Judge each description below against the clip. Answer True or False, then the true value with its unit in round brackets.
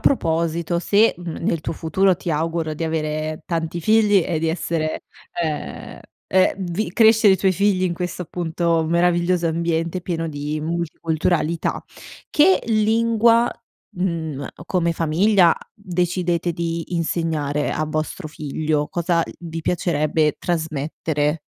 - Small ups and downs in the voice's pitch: True (2.3 semitones)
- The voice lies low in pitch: False (170 Hz)